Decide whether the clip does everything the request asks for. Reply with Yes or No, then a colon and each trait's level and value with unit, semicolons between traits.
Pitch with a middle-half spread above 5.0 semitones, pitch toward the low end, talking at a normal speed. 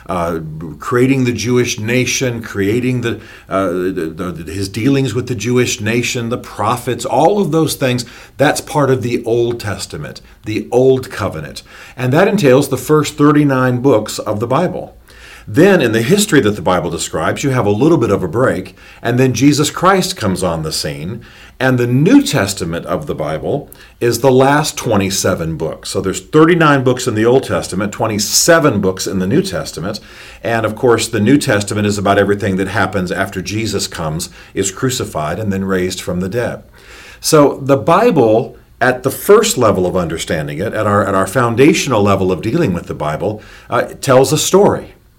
Yes: wide, 5.5 semitones; low, 120 Hz; average, 180 wpm